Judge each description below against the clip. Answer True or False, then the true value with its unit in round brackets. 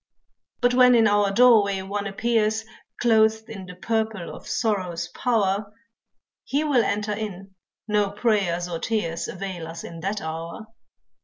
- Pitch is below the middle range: False (205 Hz)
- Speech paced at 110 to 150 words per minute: True (145 wpm)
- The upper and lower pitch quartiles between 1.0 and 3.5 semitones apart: True (2.9 semitones)